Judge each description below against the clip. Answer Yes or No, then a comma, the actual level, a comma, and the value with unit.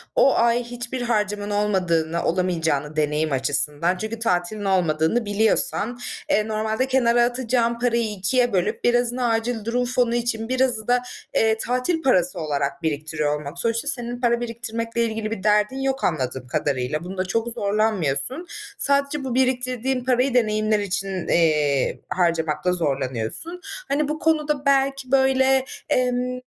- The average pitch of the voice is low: No, high, 225 Hz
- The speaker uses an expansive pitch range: Yes, wide, 5.9 semitones